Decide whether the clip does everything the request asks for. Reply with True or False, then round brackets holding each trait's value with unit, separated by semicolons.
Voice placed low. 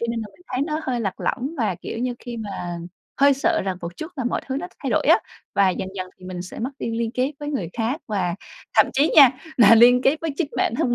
False (240 Hz)